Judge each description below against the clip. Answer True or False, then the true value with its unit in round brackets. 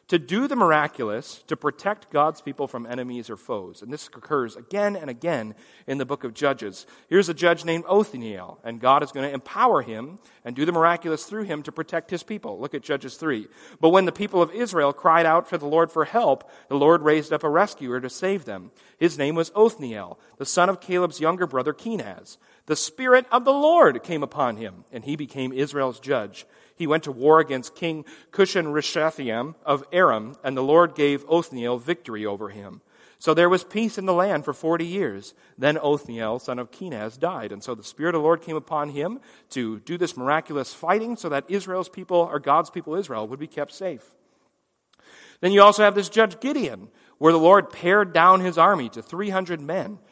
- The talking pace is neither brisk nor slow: False (210 wpm)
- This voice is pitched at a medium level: True (160 Hz)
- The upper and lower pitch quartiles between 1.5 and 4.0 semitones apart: False (4.7 semitones)